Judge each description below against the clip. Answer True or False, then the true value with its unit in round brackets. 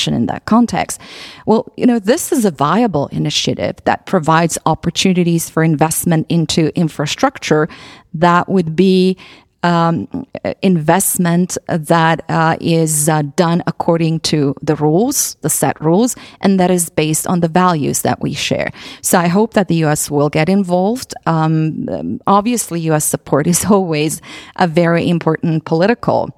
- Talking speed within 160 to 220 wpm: False (145 wpm)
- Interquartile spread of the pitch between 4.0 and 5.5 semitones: False (3.2 semitones)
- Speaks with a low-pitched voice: False (170 Hz)